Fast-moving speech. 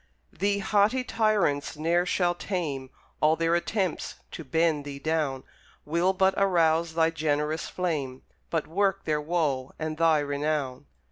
No: average, 140 wpm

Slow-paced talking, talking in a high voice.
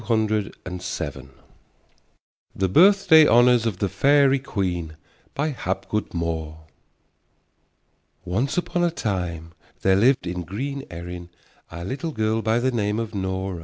No: slow, 120 wpm; low, 105 Hz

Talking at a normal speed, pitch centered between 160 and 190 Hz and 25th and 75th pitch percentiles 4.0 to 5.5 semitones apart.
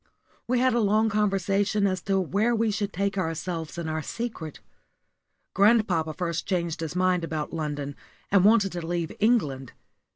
Yes: average, 160 wpm; medium, 185 Hz; average, 4.3 semitones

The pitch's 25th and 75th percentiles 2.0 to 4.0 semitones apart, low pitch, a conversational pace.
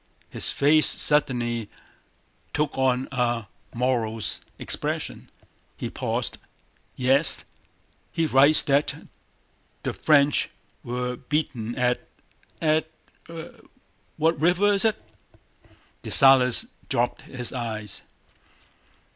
No: average, 3.7 semitones; low, 130 Hz; slow, 90 wpm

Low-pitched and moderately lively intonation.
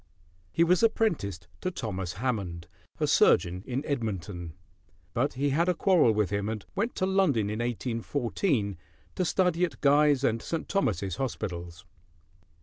No: low, 120 Hz; wide, 8.7 semitones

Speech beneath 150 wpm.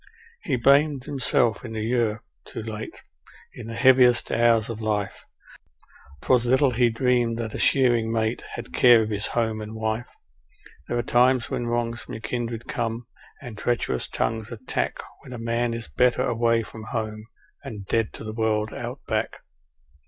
No: average, 170 wpm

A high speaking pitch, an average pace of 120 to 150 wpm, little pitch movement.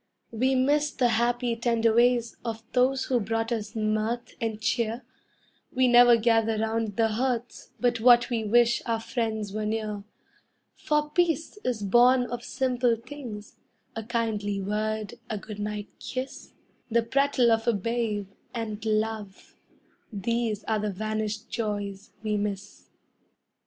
Yes: high, 225 Hz; average, 140 wpm; narrow, 2.1 semitones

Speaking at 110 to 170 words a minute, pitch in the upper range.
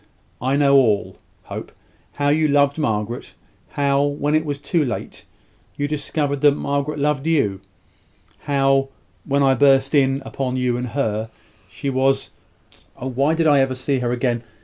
No: average, 160 wpm; medium, 140 Hz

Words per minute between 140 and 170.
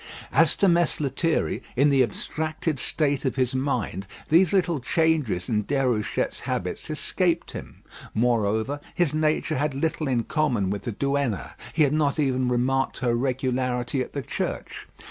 Yes: average, 155 wpm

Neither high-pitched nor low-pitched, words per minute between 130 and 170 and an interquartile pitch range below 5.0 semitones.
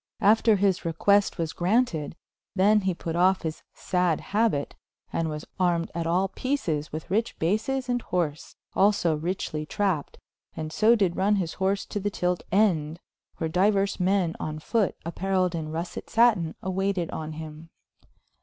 Yes: medium, 180 Hz; average, 155 wpm; average, 3.7 semitones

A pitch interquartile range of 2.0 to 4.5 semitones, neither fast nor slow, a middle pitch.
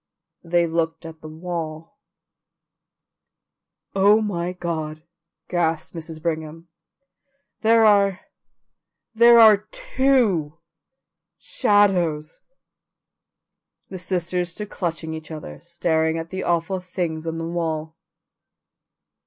No: average, 3.0 semitones; slow, 95 wpm; medium, 170 Hz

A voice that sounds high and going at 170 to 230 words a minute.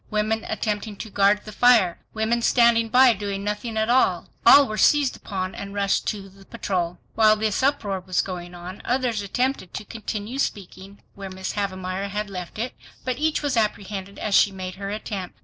Yes: high, 205 Hz; average, 190 wpm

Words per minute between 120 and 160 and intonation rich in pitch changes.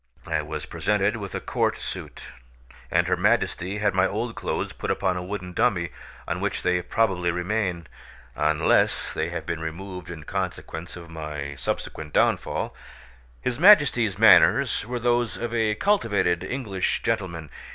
No: average, 150 wpm; average, 4.8 semitones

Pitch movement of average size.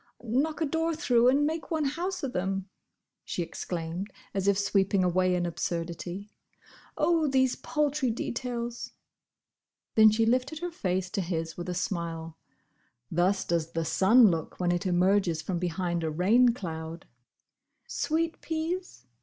No: wide, 7.1 semitones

